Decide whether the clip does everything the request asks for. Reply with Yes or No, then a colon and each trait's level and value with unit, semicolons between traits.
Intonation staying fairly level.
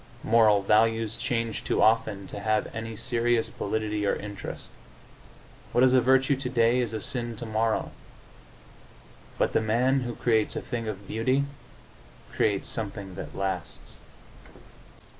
Yes: narrow, 2.2 semitones